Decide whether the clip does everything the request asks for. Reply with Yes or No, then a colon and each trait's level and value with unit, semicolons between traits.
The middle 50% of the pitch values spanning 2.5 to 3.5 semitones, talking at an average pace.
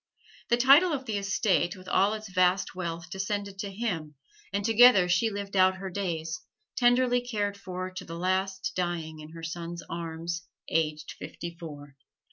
Yes: average, 3.2 semitones; average, 165 wpm